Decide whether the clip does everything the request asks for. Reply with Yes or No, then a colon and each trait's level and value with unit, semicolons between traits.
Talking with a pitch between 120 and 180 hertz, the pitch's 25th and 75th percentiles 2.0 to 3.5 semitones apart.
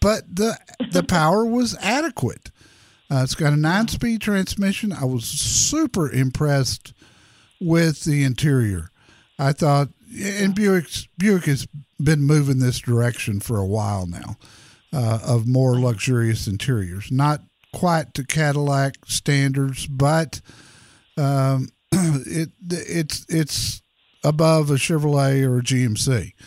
No: medium, 140 Hz; average, 5.1 semitones